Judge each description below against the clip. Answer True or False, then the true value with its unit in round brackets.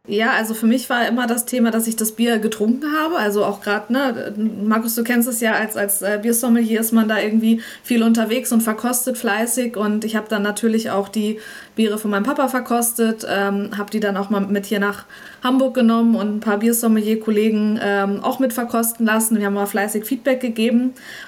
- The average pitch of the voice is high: True (225 Hz)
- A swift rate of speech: True (205 wpm)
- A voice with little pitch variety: True (2.2 semitones)